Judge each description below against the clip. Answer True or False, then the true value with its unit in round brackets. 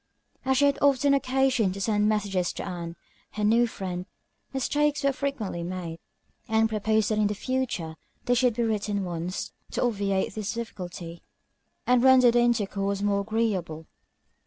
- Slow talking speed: False (155 wpm)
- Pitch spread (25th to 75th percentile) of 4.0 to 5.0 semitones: True (4.5 semitones)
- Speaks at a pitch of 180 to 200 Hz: False (215 Hz)